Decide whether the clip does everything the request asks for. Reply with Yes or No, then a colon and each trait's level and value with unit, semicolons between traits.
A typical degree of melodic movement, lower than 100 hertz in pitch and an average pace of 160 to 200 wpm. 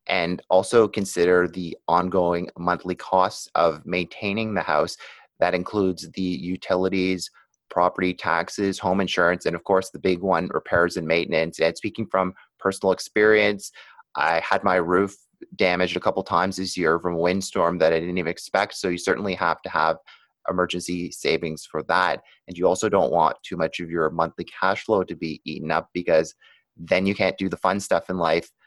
No: narrow, 1.4 semitones; very low, 90 Hz; average, 180 wpm